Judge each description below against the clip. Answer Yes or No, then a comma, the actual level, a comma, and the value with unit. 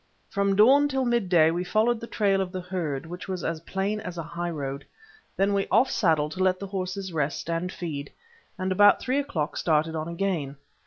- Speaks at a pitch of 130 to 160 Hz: No, medium, 185 Hz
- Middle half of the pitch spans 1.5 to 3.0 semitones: No, average, 3.5 semitones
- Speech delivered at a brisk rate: Yes, fast, 210 wpm